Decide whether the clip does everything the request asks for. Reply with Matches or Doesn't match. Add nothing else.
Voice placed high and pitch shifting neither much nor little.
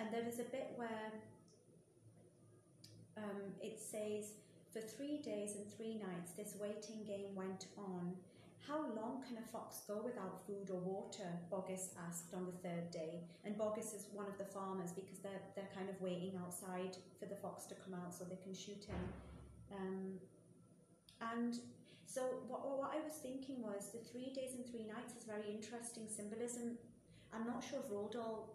Matches